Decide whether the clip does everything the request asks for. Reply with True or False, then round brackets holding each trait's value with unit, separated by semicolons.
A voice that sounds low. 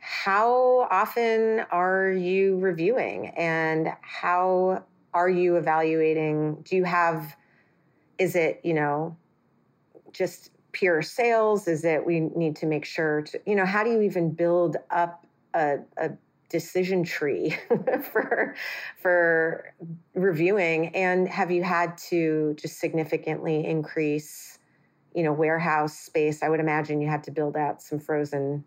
False (170 Hz)